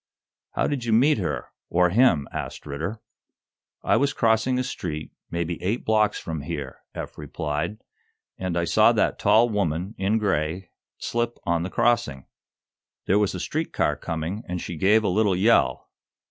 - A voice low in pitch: Yes, very low, 95 Hz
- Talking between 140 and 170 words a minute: Yes, average, 165 wpm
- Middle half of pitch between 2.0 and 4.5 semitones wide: No, average, 5.0 semitones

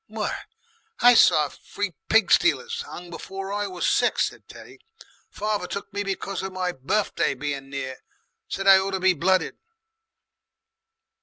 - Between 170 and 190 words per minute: No, average, 150 wpm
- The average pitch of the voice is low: No, high, 190 Hz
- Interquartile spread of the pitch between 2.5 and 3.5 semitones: Yes, average, 2.8 semitones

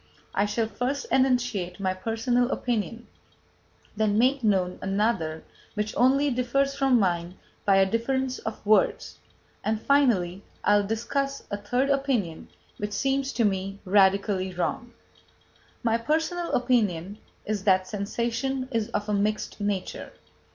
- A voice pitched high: Yes, high, 220 Hz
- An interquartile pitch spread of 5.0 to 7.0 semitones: No, average, 4.4 semitones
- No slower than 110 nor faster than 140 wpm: Yes, slow, 135 wpm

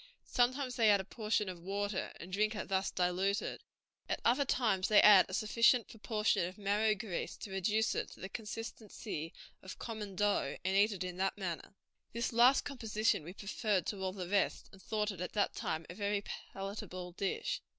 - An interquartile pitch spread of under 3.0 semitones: Yes, narrow, 2.6 semitones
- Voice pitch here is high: Yes, high, 205 Hz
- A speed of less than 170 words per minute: No, average, 190 wpm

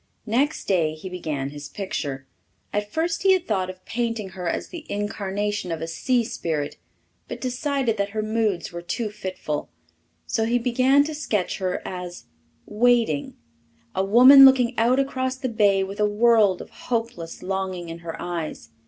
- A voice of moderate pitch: No, high, 210 Hz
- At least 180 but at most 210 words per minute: No, average, 170 wpm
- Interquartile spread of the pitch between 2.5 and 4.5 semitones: No, average, 5.2 semitones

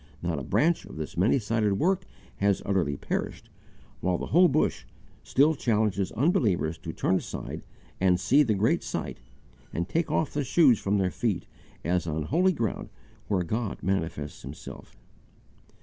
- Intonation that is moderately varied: No, wide, 7.6 semitones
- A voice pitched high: No, low, 100 Hz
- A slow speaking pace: No, average, 160 wpm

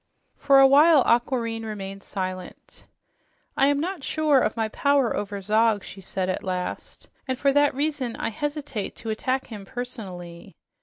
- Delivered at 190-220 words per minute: No, average, 160 wpm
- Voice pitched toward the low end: No, high, 235 Hz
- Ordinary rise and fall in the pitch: No, wide, 5.8 semitones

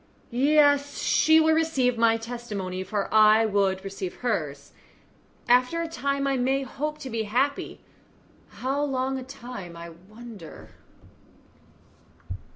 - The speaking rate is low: Yes, slow, 125 wpm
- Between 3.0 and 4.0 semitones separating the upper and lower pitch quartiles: No, average, 5.3 semitones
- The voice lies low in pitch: No, high, 245 Hz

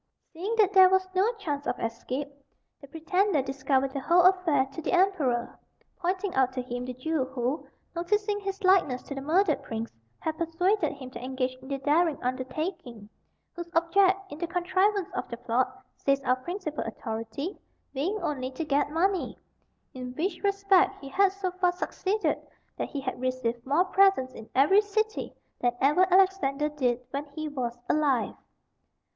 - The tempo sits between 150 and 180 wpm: Yes, average, 170 wpm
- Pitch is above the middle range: Yes, very high, 305 Hz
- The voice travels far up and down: Yes, wide, 6.4 semitones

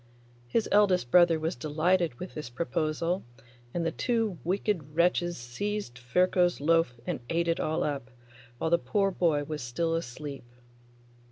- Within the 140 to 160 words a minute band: Yes, average, 150 wpm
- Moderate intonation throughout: Yes, average, 3.7 semitones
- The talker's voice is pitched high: No, medium, 165 Hz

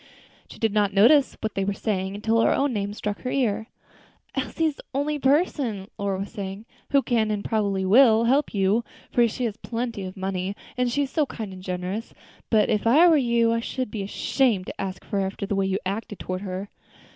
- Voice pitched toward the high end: Yes, high, 215 Hz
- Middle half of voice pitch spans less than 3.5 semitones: No, average, 3.8 semitones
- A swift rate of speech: Yes, fast, 215 wpm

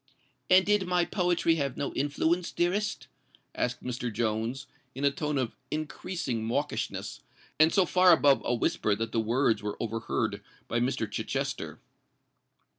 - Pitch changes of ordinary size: No, wide, 6.7 semitones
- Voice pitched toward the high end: No, medium, 140 Hz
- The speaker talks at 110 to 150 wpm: Yes, average, 145 wpm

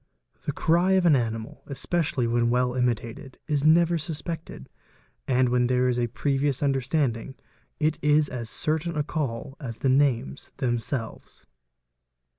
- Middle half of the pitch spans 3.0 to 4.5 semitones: Yes, average, 4.1 semitones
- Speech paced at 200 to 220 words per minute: No, average, 145 wpm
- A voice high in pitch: No, low, 135 Hz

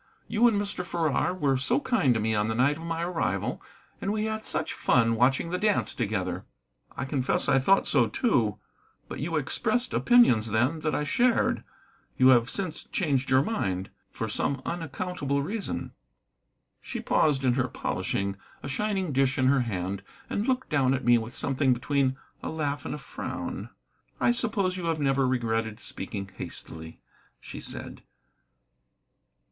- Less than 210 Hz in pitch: Yes, medium, 140 Hz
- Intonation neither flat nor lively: No, wide, 6.9 semitones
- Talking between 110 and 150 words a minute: No, average, 165 wpm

